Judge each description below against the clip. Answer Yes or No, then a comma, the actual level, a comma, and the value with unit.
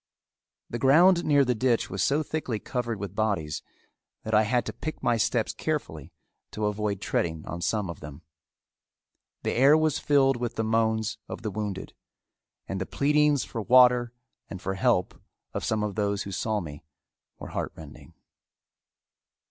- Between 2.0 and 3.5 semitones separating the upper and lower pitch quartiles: No, average, 4.7 semitones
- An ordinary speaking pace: Yes, average, 165 wpm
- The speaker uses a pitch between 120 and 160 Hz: No, low, 110 Hz